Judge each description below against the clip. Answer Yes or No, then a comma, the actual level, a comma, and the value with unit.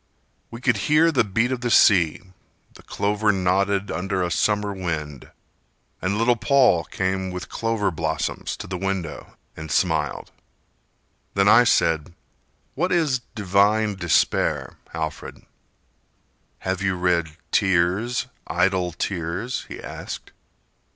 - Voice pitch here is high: No, very low, 95 Hz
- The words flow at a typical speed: No, slow, 125 wpm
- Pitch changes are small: No, average, 3.7 semitones